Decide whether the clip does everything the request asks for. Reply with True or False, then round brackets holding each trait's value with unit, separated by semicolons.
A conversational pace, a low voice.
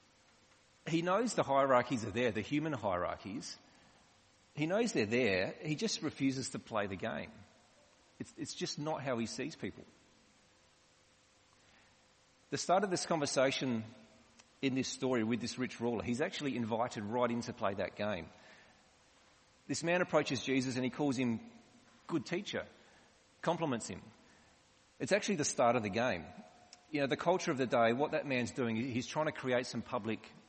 True (165 wpm; 130 Hz)